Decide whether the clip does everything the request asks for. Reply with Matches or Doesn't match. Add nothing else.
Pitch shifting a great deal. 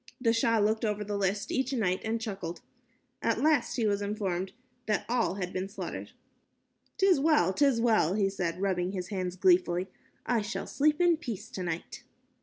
Doesn't match